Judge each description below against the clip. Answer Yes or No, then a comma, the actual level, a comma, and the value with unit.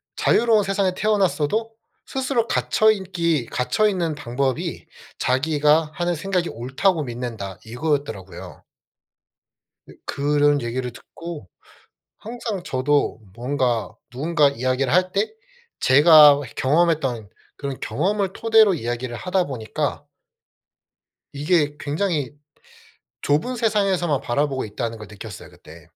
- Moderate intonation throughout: No, wide, 6.4 semitones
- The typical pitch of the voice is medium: Yes, medium, 150 Hz